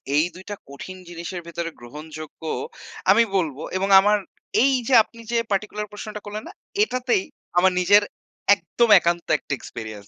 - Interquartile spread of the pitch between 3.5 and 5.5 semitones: Yes, average, 4.6 semitones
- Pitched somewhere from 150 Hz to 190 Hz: Yes, medium, 185 Hz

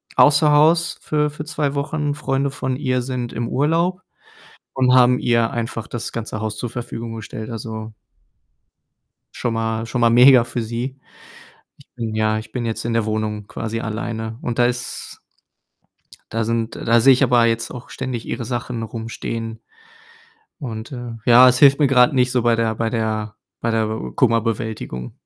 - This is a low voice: Yes, low, 120 Hz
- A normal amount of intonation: No, narrow, 2.3 semitones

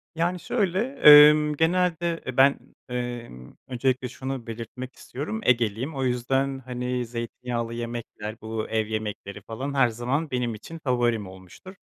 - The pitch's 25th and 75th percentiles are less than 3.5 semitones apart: Yes, average, 3.1 semitones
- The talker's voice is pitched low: Yes, low, 125 Hz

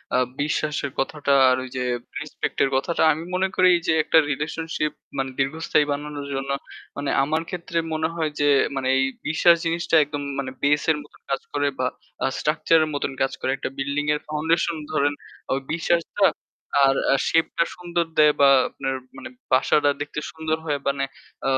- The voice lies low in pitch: No, medium, 150 Hz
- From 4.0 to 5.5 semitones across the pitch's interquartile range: No, narrow, 2.6 semitones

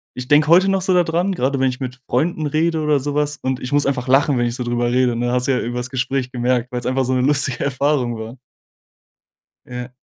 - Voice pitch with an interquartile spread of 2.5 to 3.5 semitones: Yes, average, 2.9 semitones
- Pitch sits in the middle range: No, low, 130 Hz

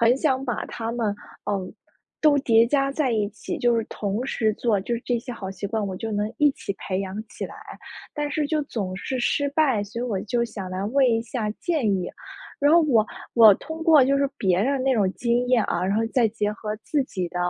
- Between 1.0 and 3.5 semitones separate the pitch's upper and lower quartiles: No, average, 4.6 semitones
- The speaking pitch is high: Yes, high, 230 Hz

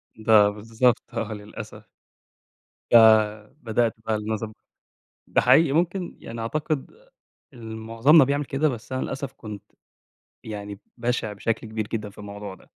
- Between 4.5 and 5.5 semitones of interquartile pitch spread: No, average, 3.8 semitones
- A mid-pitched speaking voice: No, low, 115 Hz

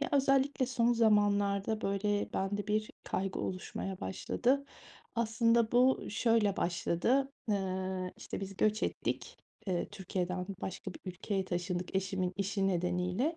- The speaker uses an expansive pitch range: No, average, 3.6 semitones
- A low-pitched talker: No, high, 200 Hz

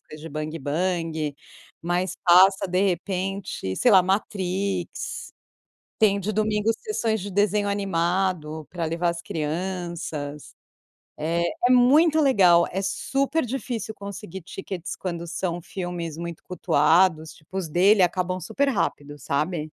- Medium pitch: Yes, medium, 180 Hz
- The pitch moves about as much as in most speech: Yes, average, 3.3 semitones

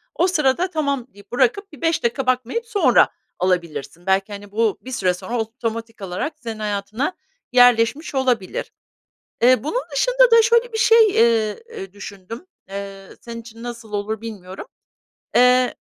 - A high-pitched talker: Yes, high, 235 Hz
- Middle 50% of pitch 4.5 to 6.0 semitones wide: Yes, wide, 5.6 semitones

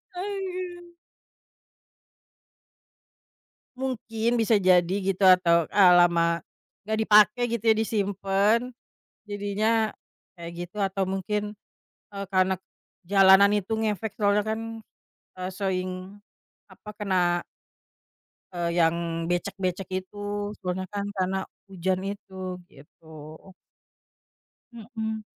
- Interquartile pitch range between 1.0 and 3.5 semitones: Yes, average, 3.0 semitones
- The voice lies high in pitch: Yes, high, 200 Hz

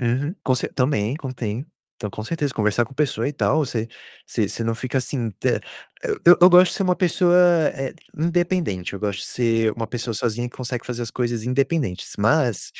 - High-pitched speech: No, low, 125 Hz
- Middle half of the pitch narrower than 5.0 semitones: No, wide, 5.4 semitones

